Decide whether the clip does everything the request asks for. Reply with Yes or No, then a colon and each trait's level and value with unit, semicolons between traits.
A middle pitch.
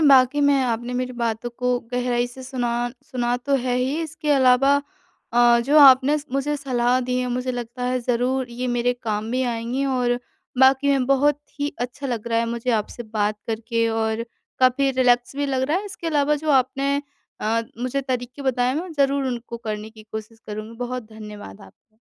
No: very high, 250 Hz